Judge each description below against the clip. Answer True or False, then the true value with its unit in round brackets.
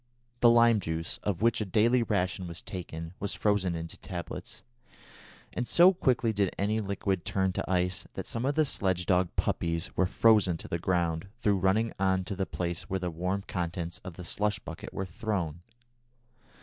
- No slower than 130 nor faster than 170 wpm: False (185 wpm)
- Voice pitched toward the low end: True (95 Hz)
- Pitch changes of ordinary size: True (3.3 semitones)